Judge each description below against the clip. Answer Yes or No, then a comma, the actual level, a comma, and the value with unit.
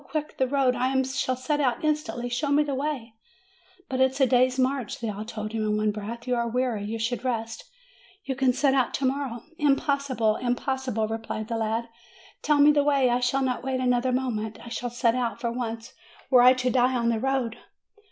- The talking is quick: Yes, fast, 220 wpm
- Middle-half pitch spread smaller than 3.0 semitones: Yes, narrow, 2.6 semitones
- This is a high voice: Yes, very high, 250 Hz